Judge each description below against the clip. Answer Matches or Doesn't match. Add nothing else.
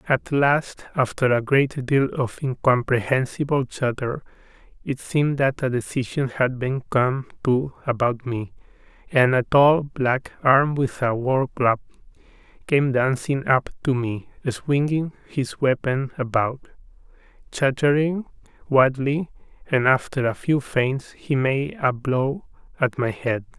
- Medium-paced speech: Doesn't match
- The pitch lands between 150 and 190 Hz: Doesn't match